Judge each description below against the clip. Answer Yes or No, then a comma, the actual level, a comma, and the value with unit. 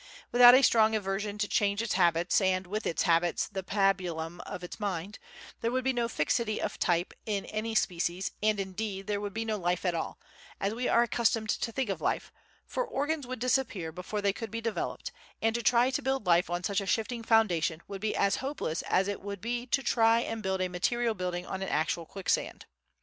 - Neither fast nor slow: No, fast, 215 wpm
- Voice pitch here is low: No, high, 205 Hz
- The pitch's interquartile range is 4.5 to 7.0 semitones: No, average, 3.9 semitones